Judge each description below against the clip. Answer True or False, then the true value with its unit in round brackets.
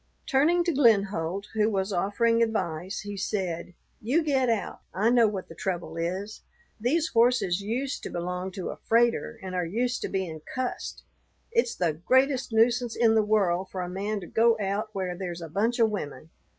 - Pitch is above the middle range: True (210 Hz)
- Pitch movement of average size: True (4.4 semitones)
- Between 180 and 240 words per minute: True (185 wpm)